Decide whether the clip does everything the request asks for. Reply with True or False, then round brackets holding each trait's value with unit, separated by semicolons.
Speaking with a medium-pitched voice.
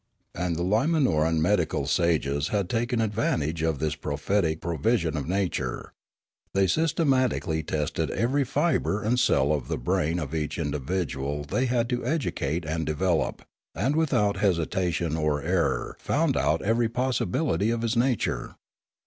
False (90 Hz)